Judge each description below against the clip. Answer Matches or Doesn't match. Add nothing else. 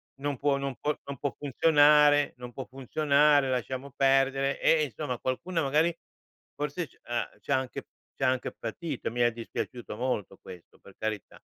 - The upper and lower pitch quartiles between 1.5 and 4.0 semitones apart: Matches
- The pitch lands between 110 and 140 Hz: Matches